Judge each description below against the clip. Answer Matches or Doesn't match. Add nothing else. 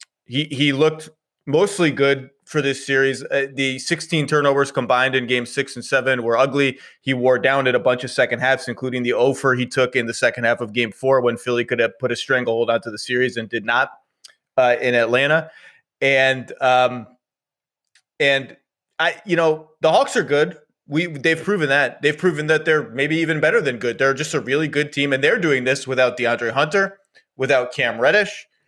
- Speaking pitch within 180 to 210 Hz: Doesn't match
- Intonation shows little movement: Doesn't match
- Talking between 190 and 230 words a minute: Matches